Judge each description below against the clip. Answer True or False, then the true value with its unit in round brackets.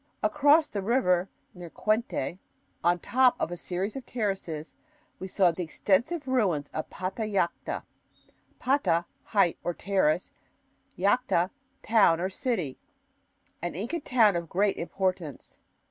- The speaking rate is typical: False (130 wpm)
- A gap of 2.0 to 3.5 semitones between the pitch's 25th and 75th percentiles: False (5.2 semitones)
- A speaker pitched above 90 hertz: True (190 Hz)